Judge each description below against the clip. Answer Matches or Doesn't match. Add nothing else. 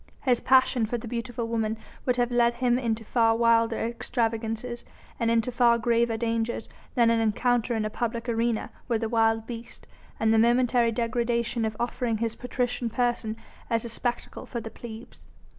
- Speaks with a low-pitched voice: Doesn't match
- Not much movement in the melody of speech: Matches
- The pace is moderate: Matches